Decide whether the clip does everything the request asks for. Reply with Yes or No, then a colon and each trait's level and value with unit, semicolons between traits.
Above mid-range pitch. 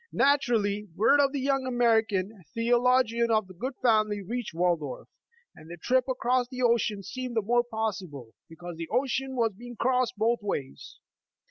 Yes: high, 230 Hz